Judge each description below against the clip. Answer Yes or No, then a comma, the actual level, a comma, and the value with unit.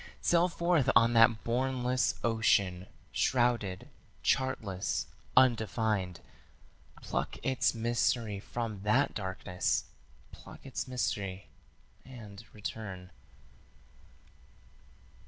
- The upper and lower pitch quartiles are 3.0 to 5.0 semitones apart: Yes, average, 4.3 semitones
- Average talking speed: No, slow, 80 wpm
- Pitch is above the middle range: No, low, 115 Hz